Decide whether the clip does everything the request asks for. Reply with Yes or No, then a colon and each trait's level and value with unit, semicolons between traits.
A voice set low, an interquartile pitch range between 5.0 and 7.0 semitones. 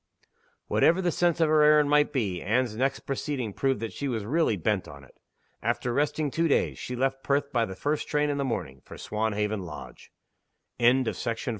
Yes: low, 130 Hz; average, 5.3 semitones